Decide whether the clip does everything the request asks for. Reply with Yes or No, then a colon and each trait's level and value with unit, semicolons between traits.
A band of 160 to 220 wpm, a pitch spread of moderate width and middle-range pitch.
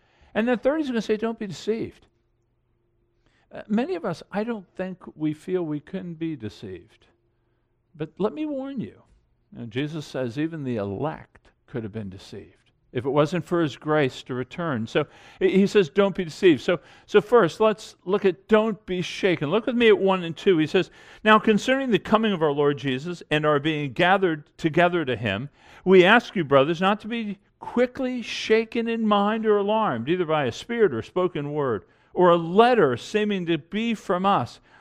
No: average, 200 wpm; wide, 6.7 semitones; medium, 175 Hz